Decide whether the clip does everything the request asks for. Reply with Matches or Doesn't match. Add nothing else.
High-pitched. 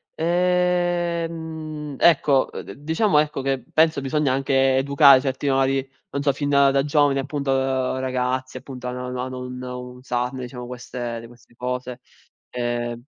Doesn't match